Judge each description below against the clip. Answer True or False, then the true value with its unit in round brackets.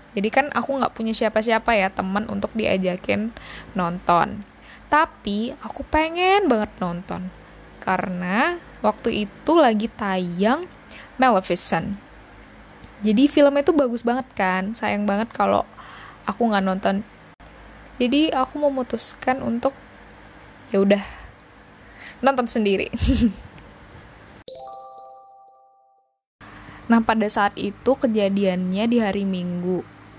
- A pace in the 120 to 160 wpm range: False (100 wpm)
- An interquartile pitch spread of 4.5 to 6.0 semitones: True (5.1 semitones)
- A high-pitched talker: True (210 Hz)